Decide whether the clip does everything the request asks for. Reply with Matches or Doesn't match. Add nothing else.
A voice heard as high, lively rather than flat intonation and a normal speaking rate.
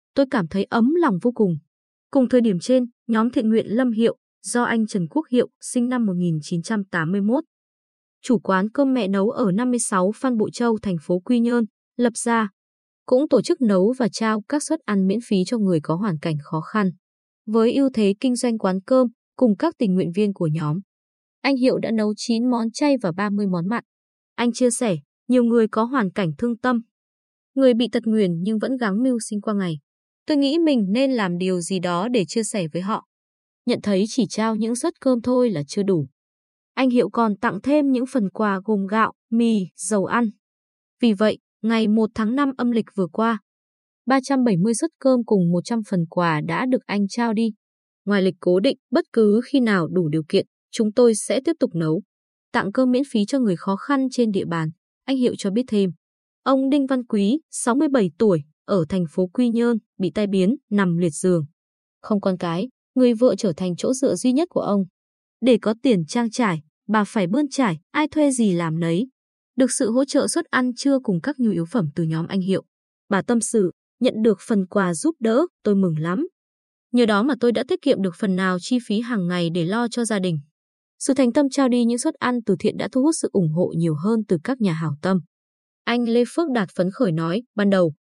Doesn't match